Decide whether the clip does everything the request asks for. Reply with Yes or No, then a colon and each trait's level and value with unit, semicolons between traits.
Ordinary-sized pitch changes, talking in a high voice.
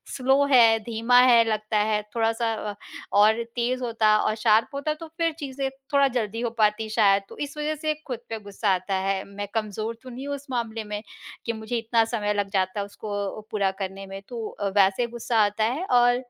Yes: average, 3.0 semitones; high, 225 Hz